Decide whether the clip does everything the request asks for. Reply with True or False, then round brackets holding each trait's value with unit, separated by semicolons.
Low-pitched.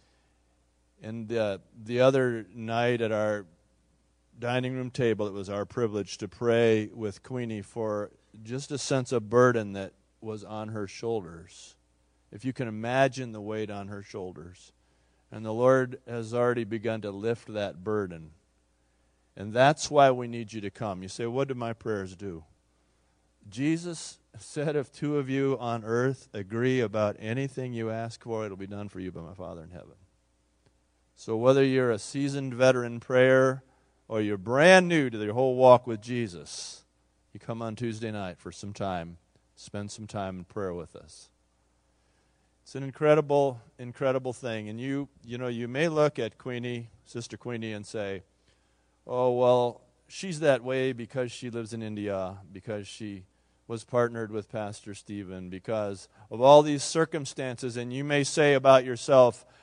True (110 Hz)